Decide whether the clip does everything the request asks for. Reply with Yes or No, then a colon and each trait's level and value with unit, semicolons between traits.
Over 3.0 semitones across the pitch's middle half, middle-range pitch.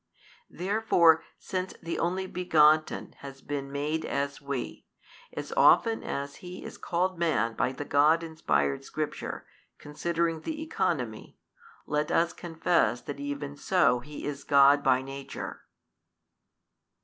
Yes: average, 3.5 semitones; medium, 150 Hz